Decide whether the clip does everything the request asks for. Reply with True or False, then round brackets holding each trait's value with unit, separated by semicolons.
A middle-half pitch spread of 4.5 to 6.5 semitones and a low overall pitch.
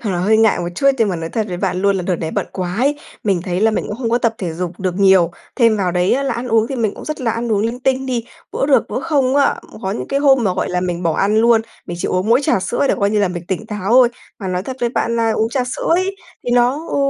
False (5.1 semitones; 220 Hz)